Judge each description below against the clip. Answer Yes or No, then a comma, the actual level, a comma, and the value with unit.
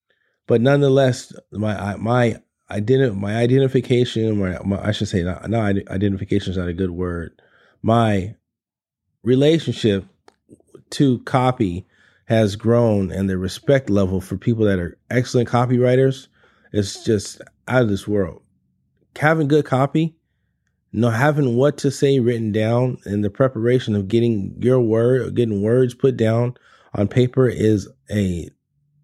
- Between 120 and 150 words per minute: Yes, slow, 135 wpm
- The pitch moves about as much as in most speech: Yes, average, 4.2 semitones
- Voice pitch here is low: Yes, low, 115 Hz